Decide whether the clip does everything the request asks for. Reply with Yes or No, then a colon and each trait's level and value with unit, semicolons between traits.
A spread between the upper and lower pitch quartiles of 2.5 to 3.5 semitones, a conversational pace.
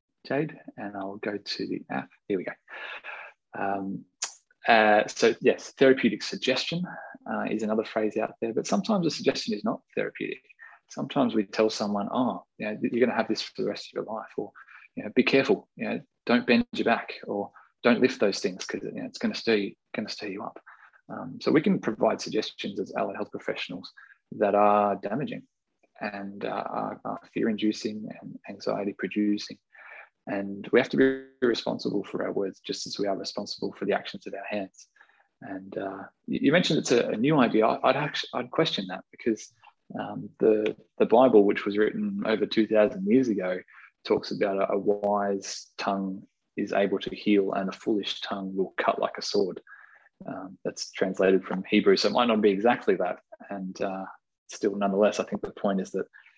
No: average, 4.3 semitones; average, 190 wpm